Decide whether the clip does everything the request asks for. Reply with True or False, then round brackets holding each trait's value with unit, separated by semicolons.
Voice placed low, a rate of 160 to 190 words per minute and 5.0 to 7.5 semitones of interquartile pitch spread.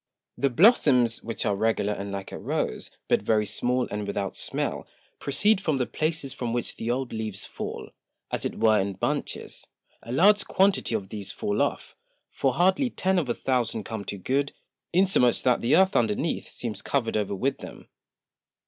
True (120 Hz; 180 wpm; 5.5 semitones)